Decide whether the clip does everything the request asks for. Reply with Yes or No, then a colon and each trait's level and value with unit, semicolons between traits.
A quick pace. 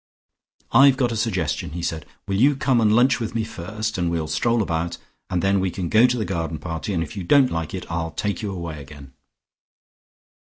Yes: fast, 220 wpm